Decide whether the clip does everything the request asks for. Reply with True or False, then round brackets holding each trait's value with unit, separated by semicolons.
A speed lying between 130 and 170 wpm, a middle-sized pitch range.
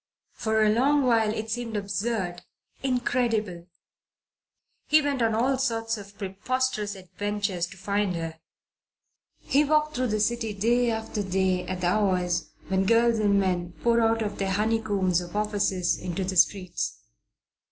True (150 wpm; 3.5 semitones)